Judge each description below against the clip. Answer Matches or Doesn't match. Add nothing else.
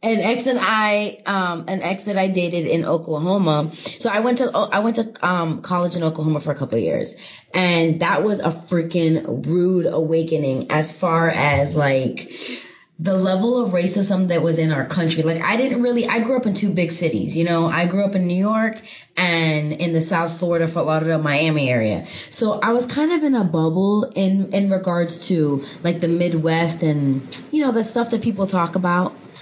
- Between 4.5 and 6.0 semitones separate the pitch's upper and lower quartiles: Doesn't match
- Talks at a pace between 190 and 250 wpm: Matches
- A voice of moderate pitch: Matches